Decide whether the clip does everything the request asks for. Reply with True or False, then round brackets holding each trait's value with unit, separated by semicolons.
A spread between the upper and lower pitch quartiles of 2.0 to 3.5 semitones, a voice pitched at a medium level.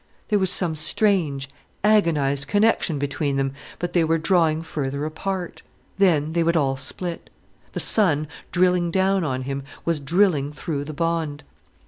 False (4.0 semitones; 160 Hz)